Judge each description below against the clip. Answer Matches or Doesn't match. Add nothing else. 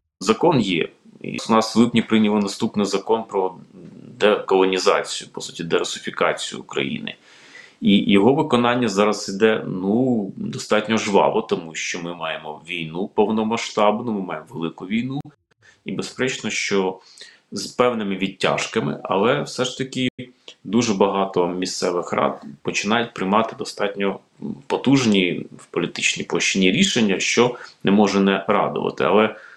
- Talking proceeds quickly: Doesn't match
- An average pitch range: Matches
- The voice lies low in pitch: Matches